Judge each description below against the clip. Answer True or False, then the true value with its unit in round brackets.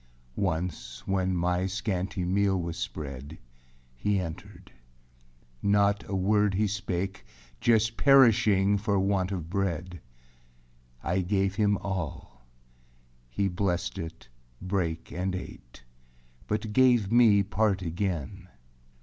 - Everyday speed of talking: False (115 wpm)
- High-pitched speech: False (95 Hz)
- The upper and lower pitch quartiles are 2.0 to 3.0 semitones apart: True (2.6 semitones)